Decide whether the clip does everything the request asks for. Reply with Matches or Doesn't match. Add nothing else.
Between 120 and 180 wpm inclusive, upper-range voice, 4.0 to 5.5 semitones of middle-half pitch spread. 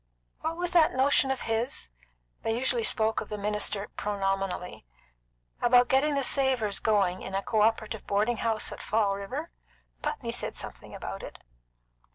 Matches